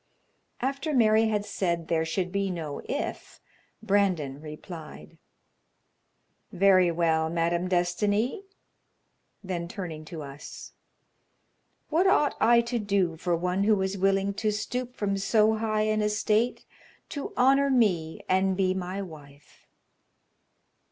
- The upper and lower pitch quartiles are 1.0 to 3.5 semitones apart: No, average, 4.1 semitones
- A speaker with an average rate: No, slow, 125 wpm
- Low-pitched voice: No, high, 195 Hz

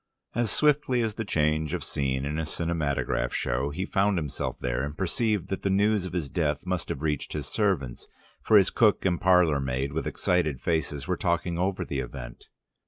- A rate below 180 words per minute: No, average, 195 wpm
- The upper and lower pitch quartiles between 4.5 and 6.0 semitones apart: Yes, average, 5.2 semitones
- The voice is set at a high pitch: No, very low, 85 Hz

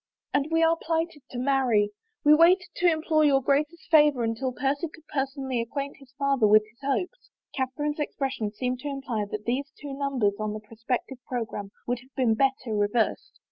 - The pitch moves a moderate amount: Yes, average, 4.0 semitones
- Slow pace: No, average, 190 wpm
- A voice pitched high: Yes, very high, 270 Hz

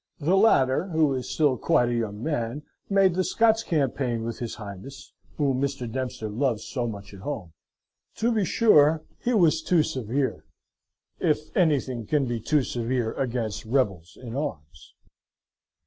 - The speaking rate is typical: Yes, average, 155 wpm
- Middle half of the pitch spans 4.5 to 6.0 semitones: Yes, average, 5.2 semitones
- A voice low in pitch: Yes, low, 130 Hz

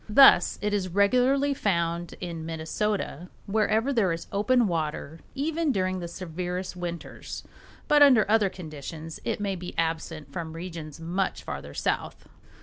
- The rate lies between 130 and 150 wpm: Yes, average, 145 wpm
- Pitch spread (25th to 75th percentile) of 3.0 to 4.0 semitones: No, average, 4.4 semitones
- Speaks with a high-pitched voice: No, medium, 180 Hz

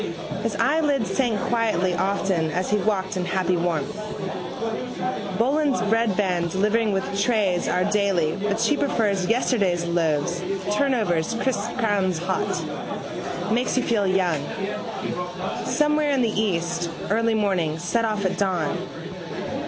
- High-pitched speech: Yes, high, 200 Hz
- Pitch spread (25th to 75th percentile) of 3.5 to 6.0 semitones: Yes, average, 4.1 semitones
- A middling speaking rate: No, slow, 125 wpm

